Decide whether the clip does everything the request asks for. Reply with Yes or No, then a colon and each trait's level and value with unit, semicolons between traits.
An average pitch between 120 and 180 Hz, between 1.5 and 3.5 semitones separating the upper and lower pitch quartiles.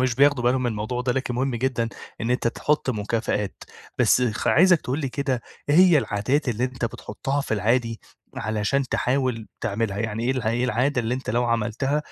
Yes: low, 125 Hz; average, 2.8 semitones